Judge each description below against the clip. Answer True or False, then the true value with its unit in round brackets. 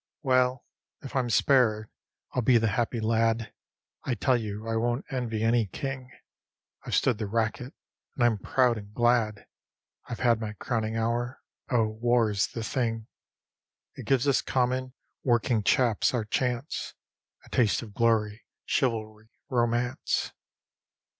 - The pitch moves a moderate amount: False (2.2 semitones)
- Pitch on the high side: False (115 Hz)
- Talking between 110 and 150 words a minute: True (140 wpm)